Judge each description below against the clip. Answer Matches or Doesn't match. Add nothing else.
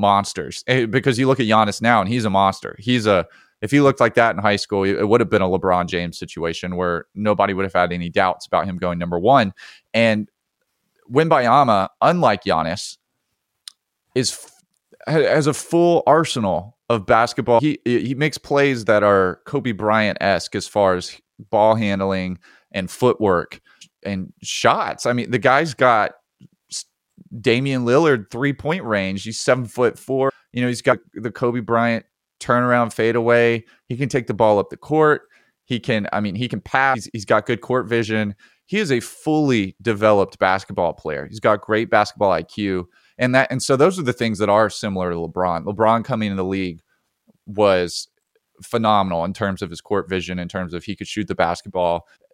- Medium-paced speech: Matches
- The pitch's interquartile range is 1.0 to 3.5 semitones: Doesn't match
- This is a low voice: Matches